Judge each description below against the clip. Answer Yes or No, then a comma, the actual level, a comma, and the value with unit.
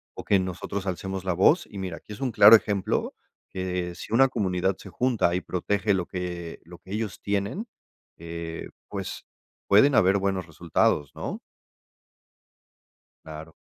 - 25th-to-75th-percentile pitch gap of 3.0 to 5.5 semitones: No, narrow, 2.6 semitones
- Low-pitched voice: Yes, very low, 95 Hz